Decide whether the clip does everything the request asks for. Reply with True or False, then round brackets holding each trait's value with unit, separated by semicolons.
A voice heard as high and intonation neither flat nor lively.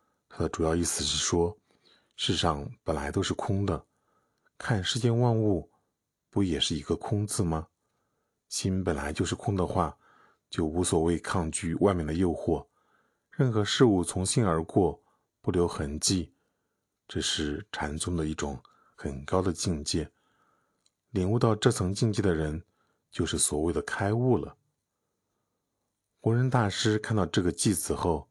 False (90 Hz; 4.7 semitones)